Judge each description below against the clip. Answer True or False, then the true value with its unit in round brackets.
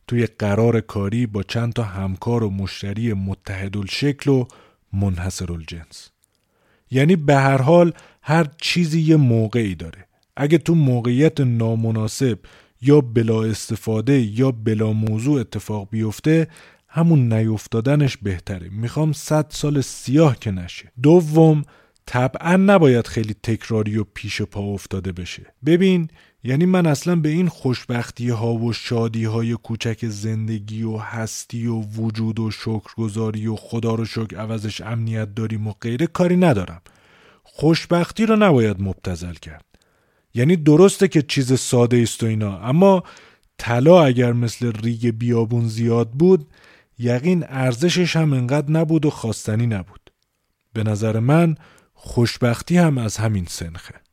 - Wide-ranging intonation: False (5.0 semitones)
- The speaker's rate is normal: True (135 wpm)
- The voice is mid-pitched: False (115 Hz)